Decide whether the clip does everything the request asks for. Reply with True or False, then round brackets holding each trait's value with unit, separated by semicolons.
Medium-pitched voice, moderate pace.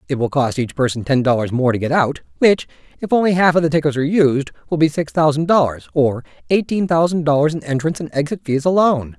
False (150 Hz; 220 wpm)